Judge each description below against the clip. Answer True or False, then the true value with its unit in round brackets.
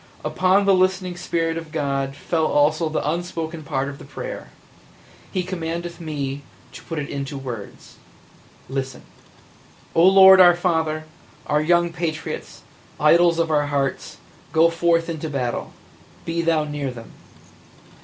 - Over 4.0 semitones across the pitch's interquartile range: False (3.1 semitones)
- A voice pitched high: False (160 Hz)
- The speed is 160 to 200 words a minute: False (145 wpm)